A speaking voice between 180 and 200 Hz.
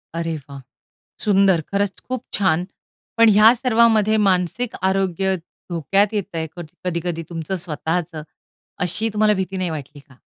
Yes: medium, 185 Hz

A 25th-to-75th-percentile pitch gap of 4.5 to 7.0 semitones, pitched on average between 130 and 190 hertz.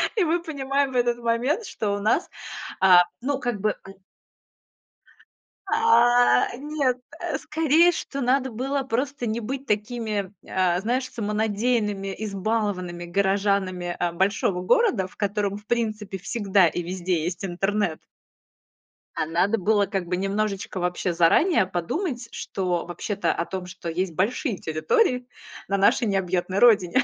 No: average, 4.9 semitones; high, 205 Hz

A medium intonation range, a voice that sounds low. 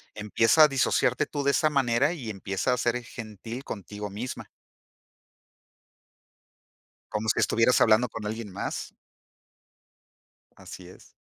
Yes: average, 3.3 semitones; low, 115 Hz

